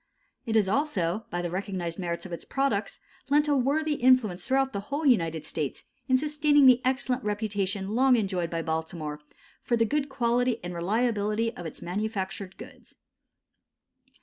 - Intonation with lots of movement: Yes, wide, 6.3 semitones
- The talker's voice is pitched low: No, high, 215 Hz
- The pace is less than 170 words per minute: Yes, average, 160 wpm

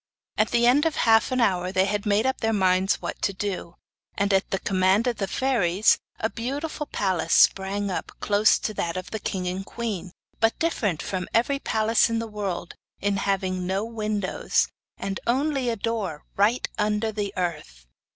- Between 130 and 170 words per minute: No, average, 185 wpm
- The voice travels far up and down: No, average, 3.3 semitones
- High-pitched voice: Yes, high, 205 Hz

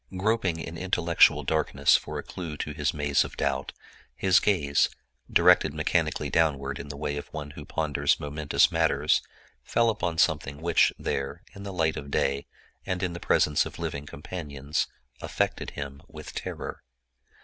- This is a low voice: Yes, very low, 75 Hz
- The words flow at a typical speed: Yes, average, 160 wpm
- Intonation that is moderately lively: Yes, average, 3.2 semitones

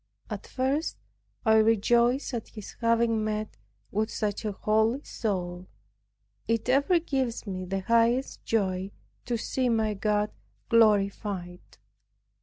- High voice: Yes, high, 220 Hz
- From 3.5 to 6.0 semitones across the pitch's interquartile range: No, narrow, 2.6 semitones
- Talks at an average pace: No, slow, 120 wpm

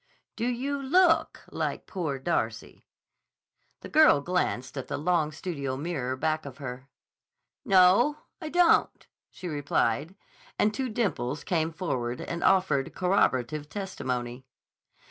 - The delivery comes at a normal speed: No, slow, 125 wpm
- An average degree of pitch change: No, wide, 6.6 semitones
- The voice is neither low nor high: Yes, medium, 160 Hz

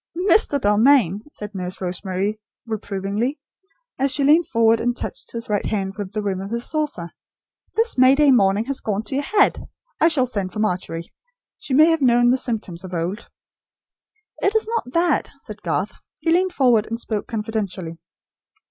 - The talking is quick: No, average, 175 wpm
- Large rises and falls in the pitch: Yes, wide, 5.9 semitones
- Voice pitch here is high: Yes, high, 225 Hz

